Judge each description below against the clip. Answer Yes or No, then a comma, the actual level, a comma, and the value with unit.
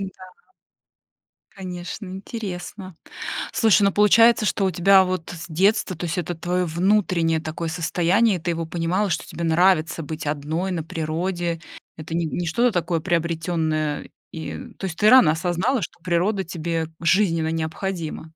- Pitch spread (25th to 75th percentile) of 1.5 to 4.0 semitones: Yes, average, 2.8 semitones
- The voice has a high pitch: No, medium, 175 Hz